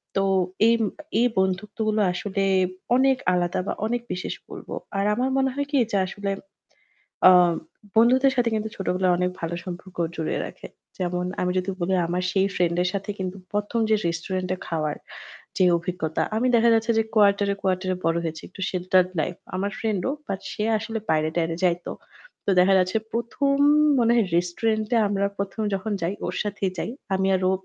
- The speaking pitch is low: No, high, 190 Hz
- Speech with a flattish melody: No, average, 3.3 semitones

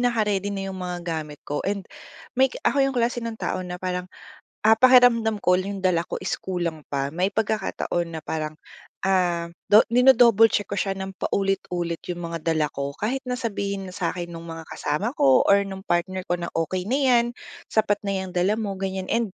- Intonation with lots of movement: No, average, 4.0 semitones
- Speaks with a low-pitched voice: No, high, 190 Hz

